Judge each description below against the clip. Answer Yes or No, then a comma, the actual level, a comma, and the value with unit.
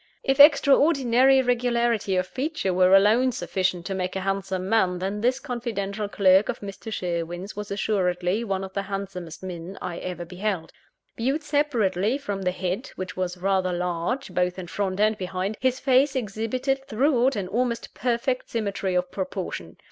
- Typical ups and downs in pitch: Yes, average, 5.0 semitones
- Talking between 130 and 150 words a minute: No, average, 165 wpm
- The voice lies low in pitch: No, high, 200 Hz